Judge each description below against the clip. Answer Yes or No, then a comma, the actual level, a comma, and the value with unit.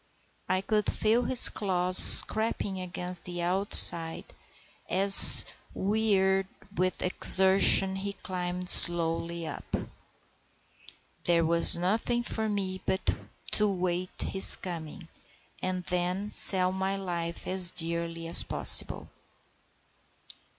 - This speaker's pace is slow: Yes, slow, 110 wpm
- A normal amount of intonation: No, narrow, 2.0 semitones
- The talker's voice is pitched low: No, medium, 185 Hz